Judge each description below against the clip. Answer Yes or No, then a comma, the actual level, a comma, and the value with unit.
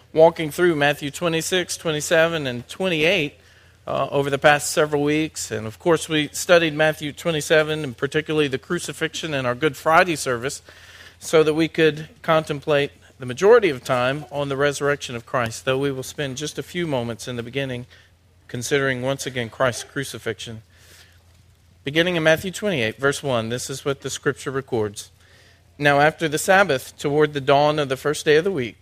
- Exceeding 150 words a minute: Yes, average, 175 wpm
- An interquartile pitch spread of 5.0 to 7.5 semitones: No, average, 4.5 semitones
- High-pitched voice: No, medium, 140 Hz